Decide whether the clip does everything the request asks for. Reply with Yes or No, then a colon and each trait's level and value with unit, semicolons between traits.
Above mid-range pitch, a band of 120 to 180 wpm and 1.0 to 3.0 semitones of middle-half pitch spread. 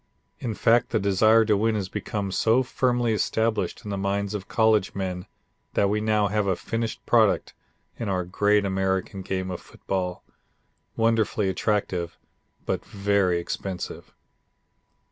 No: low, 100 Hz; average, 145 wpm; narrow, 2.6 semitones